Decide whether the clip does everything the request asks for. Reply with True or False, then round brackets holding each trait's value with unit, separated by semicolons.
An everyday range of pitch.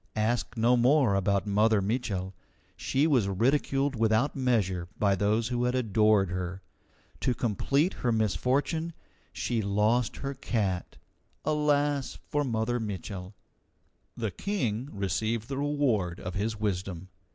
True (4.8 semitones)